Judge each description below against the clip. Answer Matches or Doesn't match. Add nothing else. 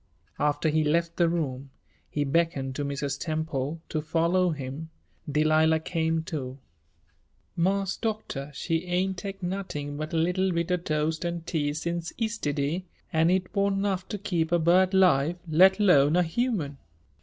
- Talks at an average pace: Matches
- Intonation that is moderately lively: Matches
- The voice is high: Doesn't match